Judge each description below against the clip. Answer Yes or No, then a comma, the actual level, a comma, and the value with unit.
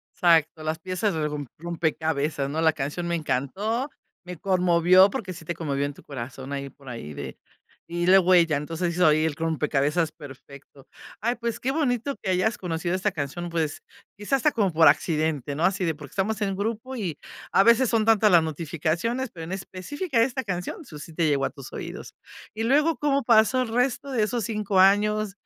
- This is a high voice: No, medium, 175 Hz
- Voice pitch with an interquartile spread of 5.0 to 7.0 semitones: Yes, wide, 5.6 semitones